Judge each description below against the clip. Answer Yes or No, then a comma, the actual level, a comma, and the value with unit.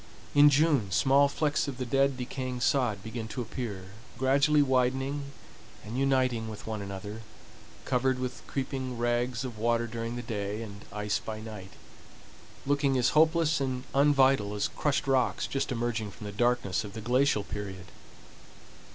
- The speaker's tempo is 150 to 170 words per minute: Yes, average, 155 wpm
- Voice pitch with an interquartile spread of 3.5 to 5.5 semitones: Yes, average, 3.8 semitones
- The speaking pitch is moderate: No, low, 125 Hz